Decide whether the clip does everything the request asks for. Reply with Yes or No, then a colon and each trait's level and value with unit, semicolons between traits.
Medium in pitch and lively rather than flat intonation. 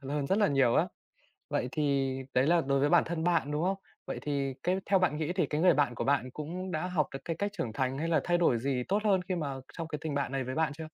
No: medium, 155 Hz; average, 4.2 semitones